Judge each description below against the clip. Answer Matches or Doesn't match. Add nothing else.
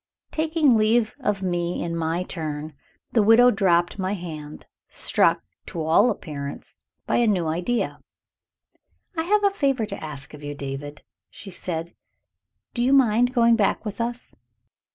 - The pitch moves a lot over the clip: Matches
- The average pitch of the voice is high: Matches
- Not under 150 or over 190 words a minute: Matches